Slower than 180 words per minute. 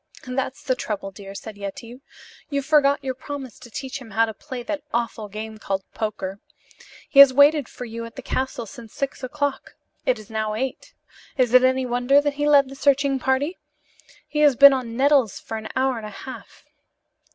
No: average, 195 wpm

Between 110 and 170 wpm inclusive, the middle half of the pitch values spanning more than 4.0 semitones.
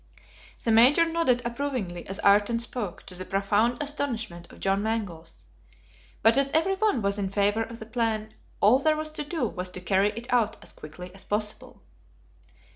No: average, 180 wpm; average, 4.5 semitones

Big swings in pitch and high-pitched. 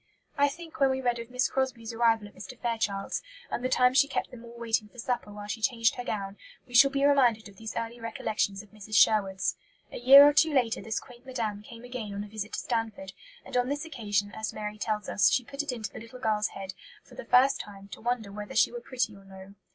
No: average, 3.3 semitones; high, 230 Hz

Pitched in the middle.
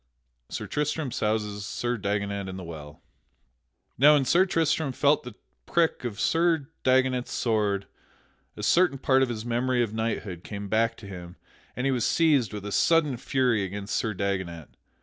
No: low, 115 Hz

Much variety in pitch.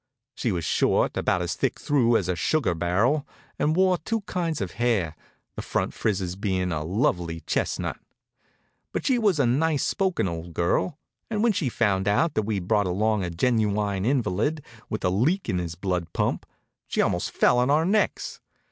Yes: wide, 8.4 semitones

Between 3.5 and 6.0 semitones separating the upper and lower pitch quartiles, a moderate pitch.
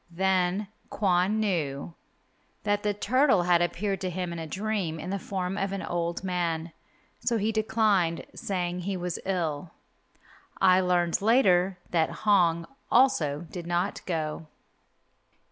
No: average, 2.7 semitones; medium, 180 Hz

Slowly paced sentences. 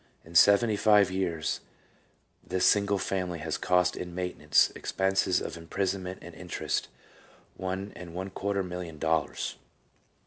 Yes: slow, 130 wpm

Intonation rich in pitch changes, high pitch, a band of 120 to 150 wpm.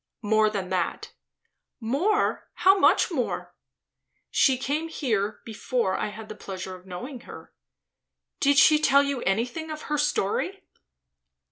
Yes: wide, 6.3 semitones; very high, 250 Hz; slow, 135 wpm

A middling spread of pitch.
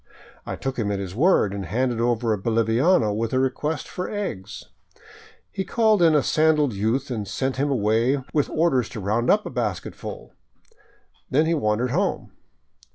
No: wide, 5.7 semitones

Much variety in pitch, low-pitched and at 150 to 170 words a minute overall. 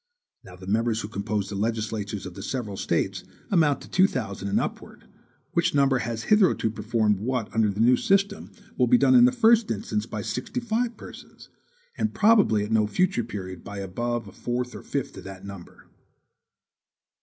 No: wide, 8.2 semitones; low, 115 Hz; average, 185 wpm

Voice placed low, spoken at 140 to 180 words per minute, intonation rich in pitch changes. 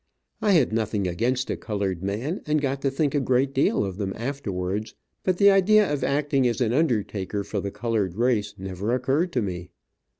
No: low, 120 Hz; average, 195 wpm; wide, 5.7 semitones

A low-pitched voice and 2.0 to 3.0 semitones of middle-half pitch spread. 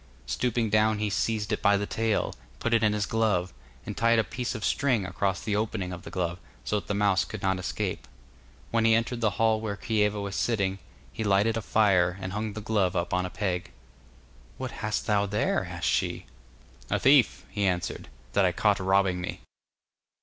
Yes: low, 105 Hz; average, 2.7 semitones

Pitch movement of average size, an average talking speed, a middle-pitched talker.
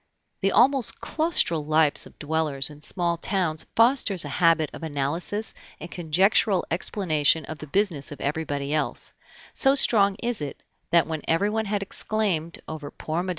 Yes: average, 4.7 semitones; average, 155 wpm; medium, 170 Hz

